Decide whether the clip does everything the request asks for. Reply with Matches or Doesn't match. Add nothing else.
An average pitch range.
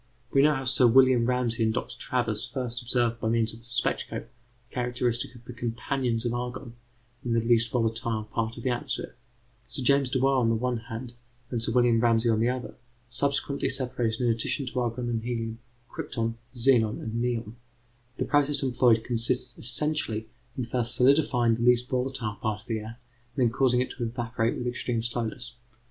Doesn't match